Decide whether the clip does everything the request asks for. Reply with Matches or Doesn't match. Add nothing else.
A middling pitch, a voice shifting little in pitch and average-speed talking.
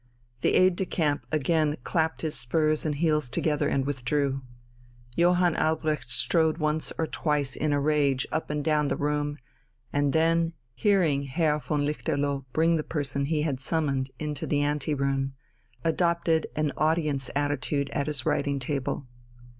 Matches